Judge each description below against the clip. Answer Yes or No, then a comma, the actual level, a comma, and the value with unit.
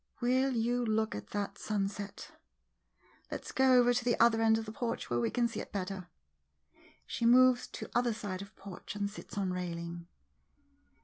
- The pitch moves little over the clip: No, average, 3.6 semitones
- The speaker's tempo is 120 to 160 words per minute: No, average, 185 wpm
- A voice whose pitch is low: No, high, 220 Hz